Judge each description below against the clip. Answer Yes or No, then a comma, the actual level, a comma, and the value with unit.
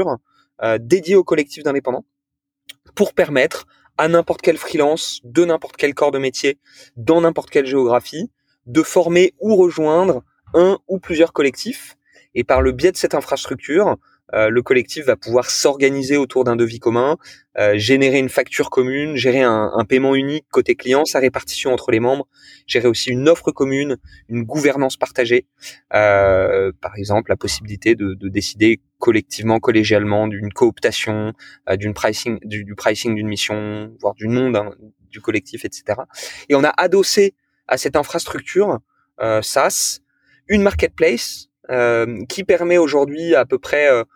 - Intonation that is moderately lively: No, wide, 6.5 semitones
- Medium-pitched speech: No, low, 130 Hz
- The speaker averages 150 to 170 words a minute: Yes, average, 160 wpm